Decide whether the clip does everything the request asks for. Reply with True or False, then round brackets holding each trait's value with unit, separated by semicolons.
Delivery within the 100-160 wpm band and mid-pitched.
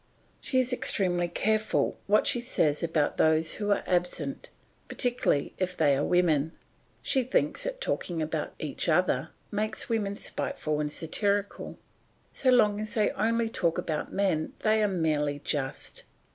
True (150 wpm; 180 Hz)